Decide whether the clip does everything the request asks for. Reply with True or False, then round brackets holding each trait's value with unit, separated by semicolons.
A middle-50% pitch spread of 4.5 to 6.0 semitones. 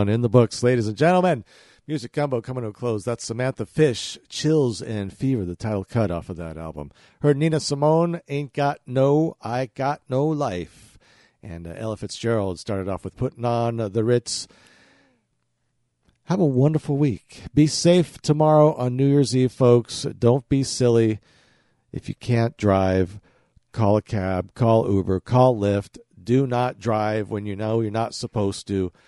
True (5.1 semitones)